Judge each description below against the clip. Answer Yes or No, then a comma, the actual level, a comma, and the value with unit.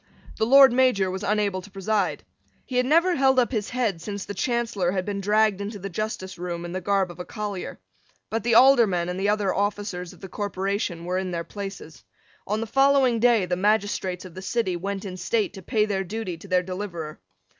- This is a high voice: Yes, high, 200 Hz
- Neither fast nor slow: No, fast, 215 wpm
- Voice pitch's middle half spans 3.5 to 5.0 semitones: No, average, 3.1 semitones